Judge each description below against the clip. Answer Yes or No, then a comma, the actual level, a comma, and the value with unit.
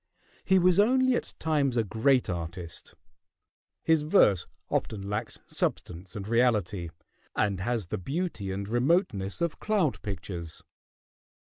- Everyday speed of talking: No, slow, 125 wpm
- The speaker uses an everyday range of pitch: No, wide, 8.9 semitones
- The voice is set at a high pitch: No, low, 110 Hz